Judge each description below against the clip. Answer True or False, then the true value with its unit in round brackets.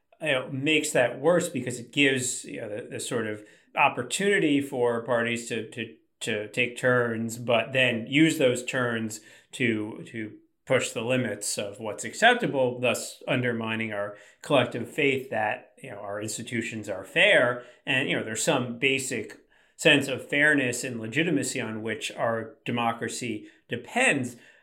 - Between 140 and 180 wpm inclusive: True (155 wpm)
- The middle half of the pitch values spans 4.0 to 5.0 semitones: False (3.0 semitones)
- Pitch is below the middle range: True (125 Hz)